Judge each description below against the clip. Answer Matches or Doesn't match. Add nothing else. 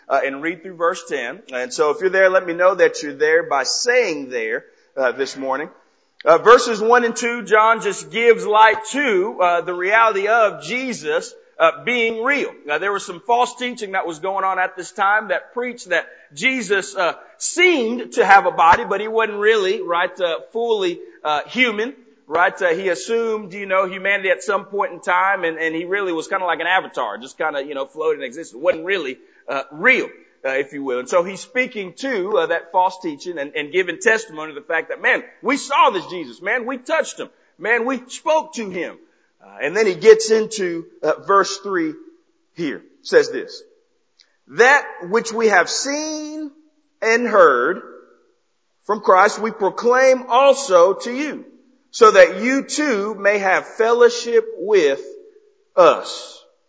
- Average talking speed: Matches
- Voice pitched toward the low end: Doesn't match